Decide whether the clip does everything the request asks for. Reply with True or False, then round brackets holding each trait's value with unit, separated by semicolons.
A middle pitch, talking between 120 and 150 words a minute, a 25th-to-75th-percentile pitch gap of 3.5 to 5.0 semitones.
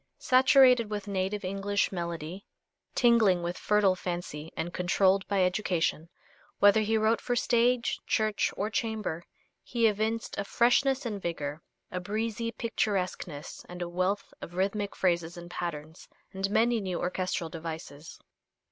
False (195 Hz; 140 wpm; 4.1 semitones)